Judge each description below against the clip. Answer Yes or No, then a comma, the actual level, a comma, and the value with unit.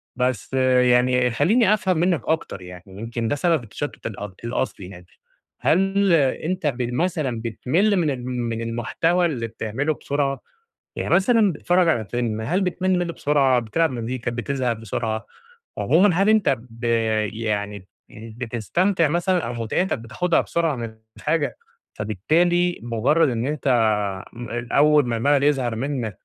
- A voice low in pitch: Yes, low, 130 Hz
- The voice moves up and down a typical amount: No, wide, 6.4 semitones